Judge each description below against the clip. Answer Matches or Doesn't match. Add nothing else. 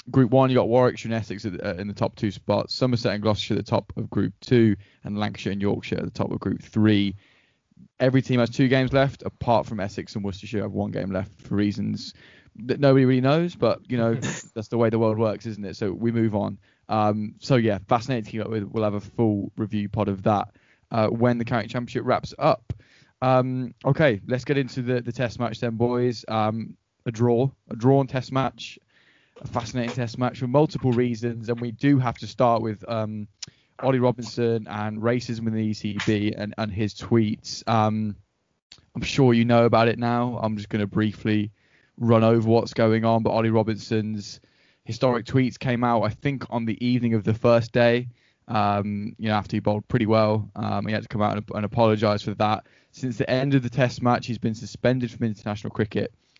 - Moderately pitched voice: Doesn't match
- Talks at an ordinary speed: Doesn't match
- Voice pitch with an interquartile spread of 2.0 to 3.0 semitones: Matches